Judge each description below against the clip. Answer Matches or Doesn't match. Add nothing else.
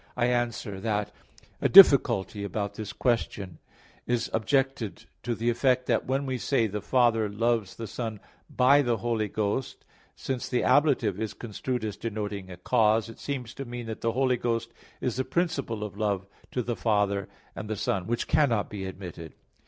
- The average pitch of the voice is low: Matches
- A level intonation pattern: Doesn't match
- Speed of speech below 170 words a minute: Doesn't match